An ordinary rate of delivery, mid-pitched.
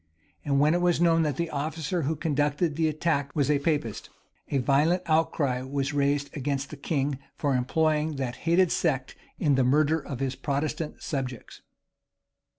Yes: average, 165 wpm; medium, 145 Hz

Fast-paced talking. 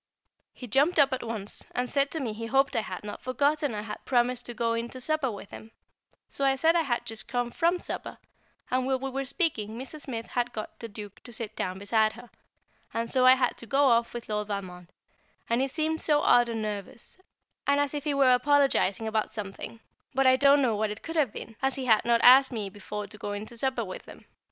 Yes: fast, 240 wpm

